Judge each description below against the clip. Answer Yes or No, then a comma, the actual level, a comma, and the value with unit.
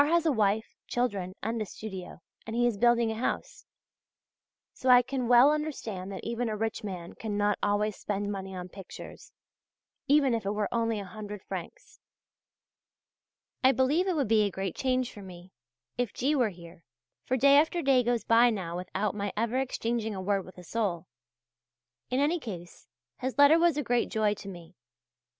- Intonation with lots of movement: No, average, 4.5 semitones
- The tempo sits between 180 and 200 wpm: Yes, average, 185 wpm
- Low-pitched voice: No, high, 220 Hz